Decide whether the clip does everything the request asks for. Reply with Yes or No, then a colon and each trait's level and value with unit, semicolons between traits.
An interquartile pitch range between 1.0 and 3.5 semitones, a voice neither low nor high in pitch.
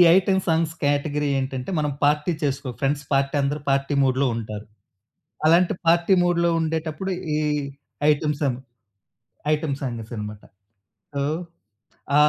Yes: average, 3.0 semitones; medium, 145 Hz